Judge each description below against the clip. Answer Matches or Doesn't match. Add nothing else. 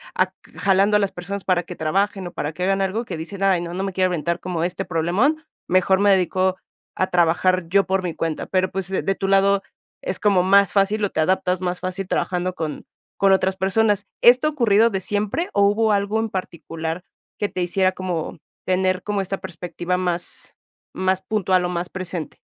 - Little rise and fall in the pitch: Matches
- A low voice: Doesn't match